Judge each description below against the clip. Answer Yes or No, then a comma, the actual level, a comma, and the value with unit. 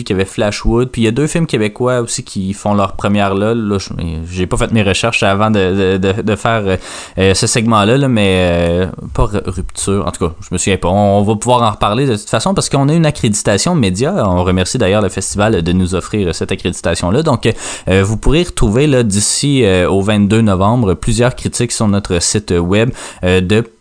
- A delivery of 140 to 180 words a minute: No, average, 215 wpm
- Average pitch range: Yes, average, 3.8 semitones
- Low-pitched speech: Yes, low, 105 Hz